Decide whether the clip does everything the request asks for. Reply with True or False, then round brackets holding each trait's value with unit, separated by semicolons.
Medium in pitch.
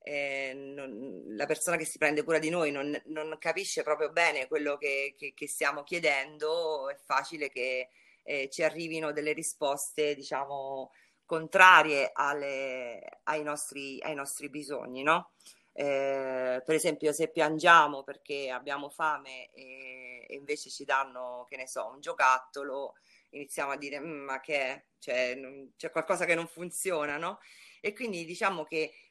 True (145 Hz)